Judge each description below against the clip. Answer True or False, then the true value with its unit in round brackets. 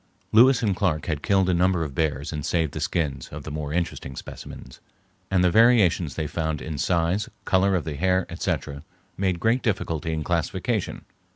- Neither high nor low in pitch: False (85 Hz)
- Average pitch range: True (3.6 semitones)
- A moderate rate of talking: True (185 wpm)